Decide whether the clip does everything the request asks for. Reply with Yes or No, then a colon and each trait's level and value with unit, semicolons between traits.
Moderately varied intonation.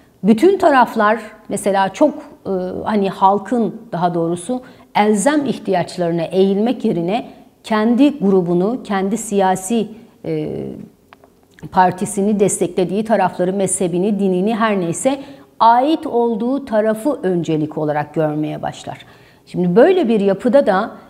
Yes: average, 4.3 semitones